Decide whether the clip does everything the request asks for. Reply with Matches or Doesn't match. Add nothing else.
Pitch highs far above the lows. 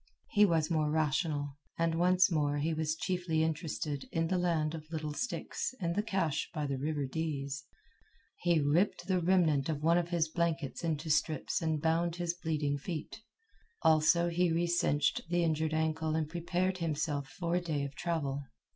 Doesn't match